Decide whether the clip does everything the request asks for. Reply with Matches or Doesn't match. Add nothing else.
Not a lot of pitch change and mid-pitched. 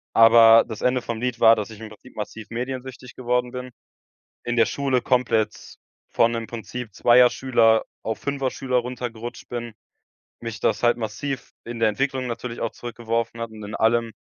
Doesn't match